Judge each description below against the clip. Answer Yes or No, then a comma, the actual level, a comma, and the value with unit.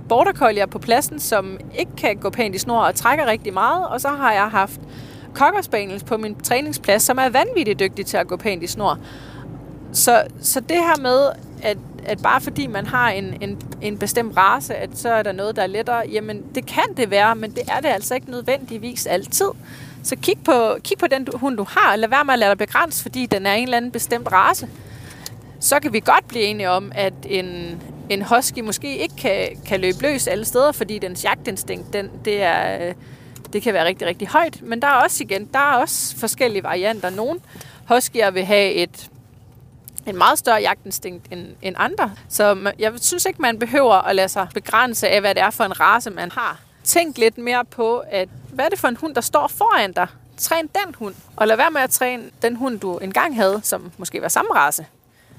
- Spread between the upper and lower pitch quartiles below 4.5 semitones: No, average, 4.8 semitones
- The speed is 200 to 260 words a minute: Yes, average, 220 wpm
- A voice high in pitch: Yes, high, 215 Hz